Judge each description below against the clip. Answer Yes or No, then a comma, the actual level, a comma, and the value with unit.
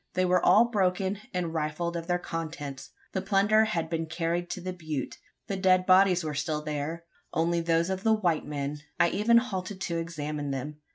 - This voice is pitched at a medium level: Yes, medium, 170 Hz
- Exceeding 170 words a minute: Yes, average, 190 wpm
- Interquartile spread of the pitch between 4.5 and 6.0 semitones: No, average, 3.3 semitones